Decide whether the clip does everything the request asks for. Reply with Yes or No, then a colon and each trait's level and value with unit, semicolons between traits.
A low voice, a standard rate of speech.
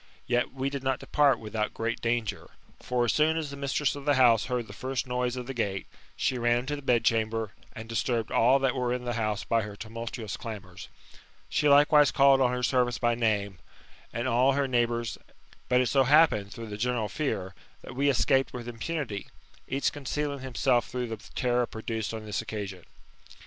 Yes: low, 120 Hz; average, 195 wpm